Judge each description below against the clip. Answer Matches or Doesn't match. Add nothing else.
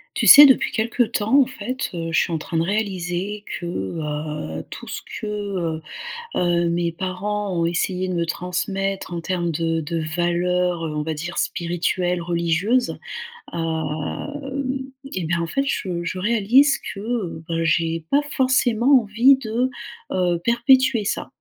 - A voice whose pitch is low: Doesn't match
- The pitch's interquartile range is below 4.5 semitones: Doesn't match